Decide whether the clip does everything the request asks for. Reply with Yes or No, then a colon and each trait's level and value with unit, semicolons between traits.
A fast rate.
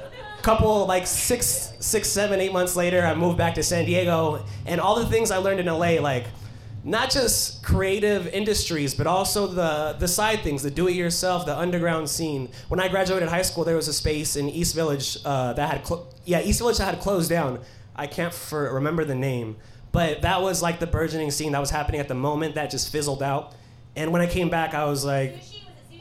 Yes: fast, 210 wpm